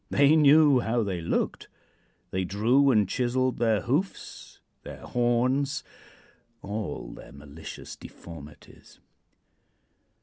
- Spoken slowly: Yes, slow, 100 wpm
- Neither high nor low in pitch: No, low, 120 Hz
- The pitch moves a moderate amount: No, wide, 5.8 semitones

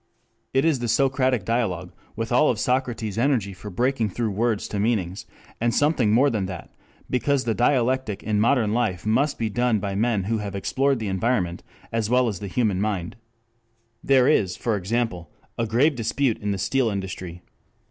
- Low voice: Yes, low, 115 Hz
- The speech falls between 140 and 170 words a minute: No, average, 180 wpm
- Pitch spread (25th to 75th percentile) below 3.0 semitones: No, average, 3.9 semitones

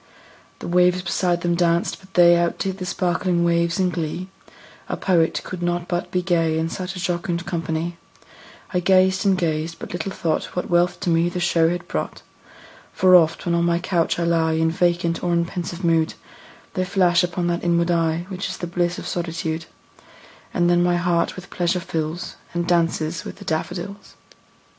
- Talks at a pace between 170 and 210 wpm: Yes, average, 190 wpm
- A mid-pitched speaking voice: Yes, medium, 175 Hz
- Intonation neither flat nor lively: No, narrow, 1.2 semitones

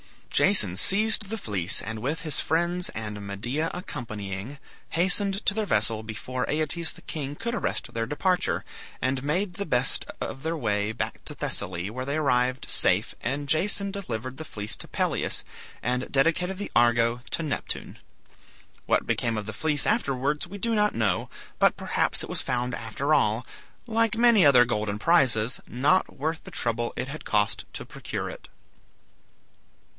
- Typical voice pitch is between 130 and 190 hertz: Yes, low, 135 Hz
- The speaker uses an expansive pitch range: Yes, wide, 7.4 semitones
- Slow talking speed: No, average, 165 wpm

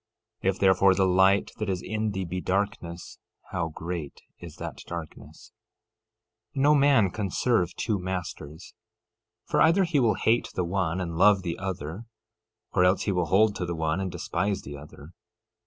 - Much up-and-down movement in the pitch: No, average, 3.2 semitones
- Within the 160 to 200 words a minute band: Yes, average, 170 wpm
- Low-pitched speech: Yes, very low, 95 Hz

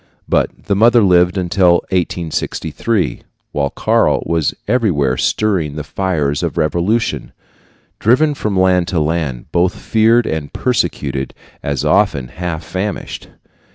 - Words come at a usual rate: No, slow, 120 wpm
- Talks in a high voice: No, very low, 90 Hz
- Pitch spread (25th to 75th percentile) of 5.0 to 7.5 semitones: Yes, average, 5.3 semitones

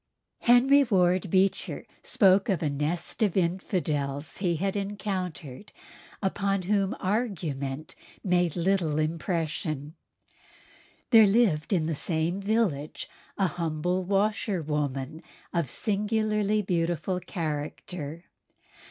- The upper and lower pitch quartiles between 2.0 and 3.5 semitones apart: No, average, 4.2 semitones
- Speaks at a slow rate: Yes, slow, 100 wpm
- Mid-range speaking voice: Yes, medium, 180 Hz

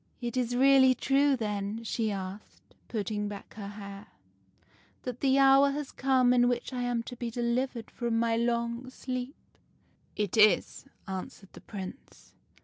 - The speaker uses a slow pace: No, average, 170 wpm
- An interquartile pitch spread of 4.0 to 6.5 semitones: No, average, 3.3 semitones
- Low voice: No, high, 235 Hz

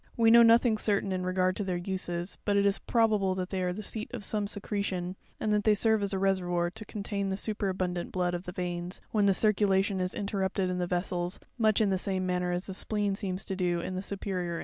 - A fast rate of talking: Yes, fast, 240 wpm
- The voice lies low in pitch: No, high, 190 Hz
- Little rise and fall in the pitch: Yes, narrow, 2.2 semitones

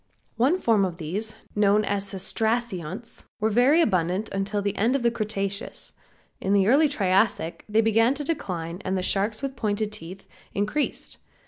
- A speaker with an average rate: Yes, average, 160 wpm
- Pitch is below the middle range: No, high, 210 Hz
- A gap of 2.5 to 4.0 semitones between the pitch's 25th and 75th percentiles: Yes, average, 3.2 semitones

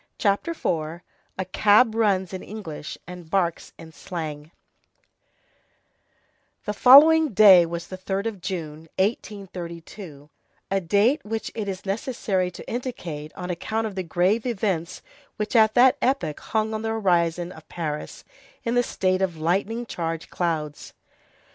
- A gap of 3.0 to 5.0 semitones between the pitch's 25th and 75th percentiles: Yes, average, 4.5 semitones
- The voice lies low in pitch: No, high, 190 Hz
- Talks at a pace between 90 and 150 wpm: Yes, average, 140 wpm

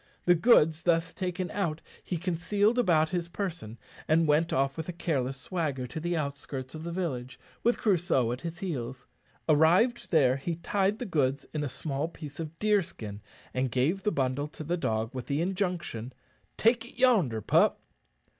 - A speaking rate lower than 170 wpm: No, average, 175 wpm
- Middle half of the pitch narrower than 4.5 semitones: No, average, 5.0 semitones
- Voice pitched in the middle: Yes, medium, 160 Hz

